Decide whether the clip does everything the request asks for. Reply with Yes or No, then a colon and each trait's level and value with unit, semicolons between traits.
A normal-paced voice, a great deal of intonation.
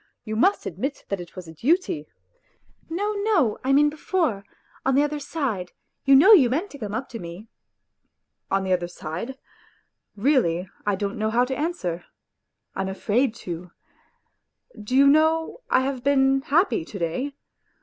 Yes: average, 180 wpm; wide, 7.3 semitones